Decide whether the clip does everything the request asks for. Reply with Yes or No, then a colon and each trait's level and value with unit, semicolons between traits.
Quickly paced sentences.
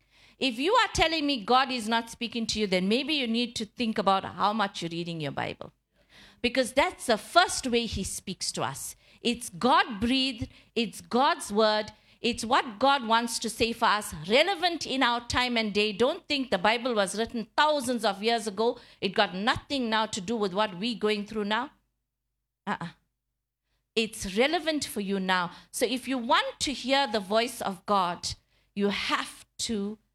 No: average, 185 wpm